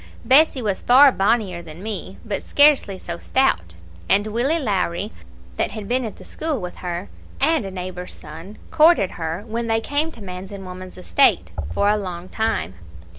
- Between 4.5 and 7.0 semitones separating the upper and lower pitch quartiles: Yes, average, 5.1 semitones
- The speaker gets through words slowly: No, average, 180 wpm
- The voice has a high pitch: Yes, high, 200 Hz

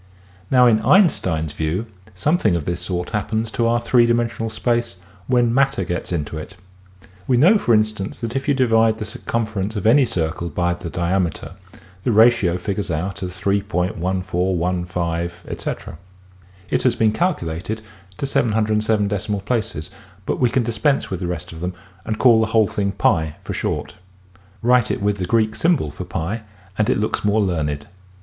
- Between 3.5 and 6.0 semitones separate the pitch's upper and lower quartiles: Yes, average, 4.7 semitones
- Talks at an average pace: Yes, average, 165 wpm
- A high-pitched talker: No, low, 105 Hz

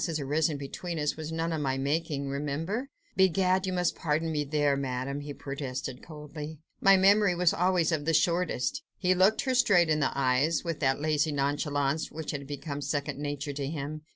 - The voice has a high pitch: No, medium, 150 Hz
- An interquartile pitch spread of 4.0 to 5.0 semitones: No, average, 3.2 semitones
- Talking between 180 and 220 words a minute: Yes, average, 190 wpm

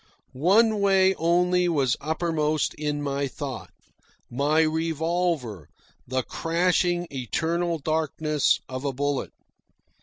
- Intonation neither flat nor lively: Yes, average, 3.7 semitones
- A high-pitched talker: No, medium, 155 Hz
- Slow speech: Yes, slow, 100 wpm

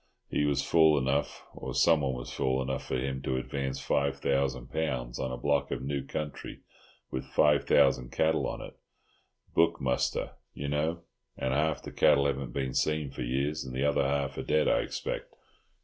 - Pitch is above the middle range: No, very low, 70 Hz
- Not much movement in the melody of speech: Yes, narrow, 2.1 semitones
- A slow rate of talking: No, average, 180 wpm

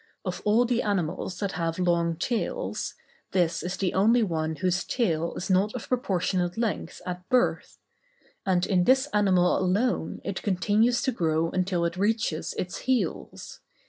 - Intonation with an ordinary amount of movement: Yes, average, 3.8 semitones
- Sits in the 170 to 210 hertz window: Yes, medium, 185 Hz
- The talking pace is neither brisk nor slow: Yes, average, 155 wpm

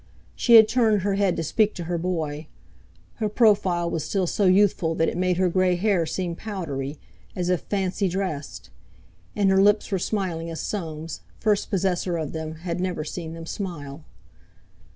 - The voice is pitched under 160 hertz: No, medium, 180 Hz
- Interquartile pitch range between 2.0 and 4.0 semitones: Yes, average, 3.3 semitones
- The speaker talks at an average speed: Yes, average, 175 wpm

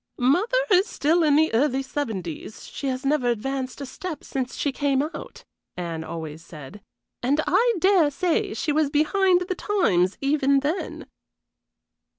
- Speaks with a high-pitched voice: Yes, very high, 280 Hz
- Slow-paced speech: No, average, 155 wpm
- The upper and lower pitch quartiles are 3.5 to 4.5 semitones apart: No, average, 5.1 semitones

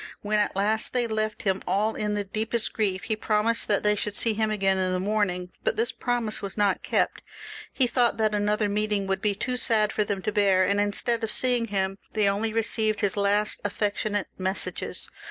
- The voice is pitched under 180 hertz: No, high, 210 Hz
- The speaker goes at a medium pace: No, fast, 210 wpm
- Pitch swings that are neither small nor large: No, narrow, 1.6 semitones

